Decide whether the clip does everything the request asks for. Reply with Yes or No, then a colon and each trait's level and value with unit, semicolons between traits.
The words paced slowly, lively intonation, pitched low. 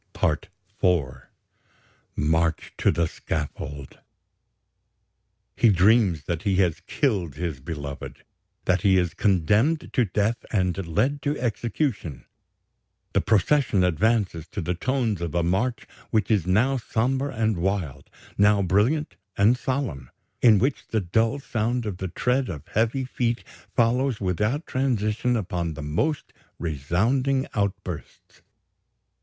Yes: slow, 125 wpm; wide, 6.0 semitones; low, 100 Hz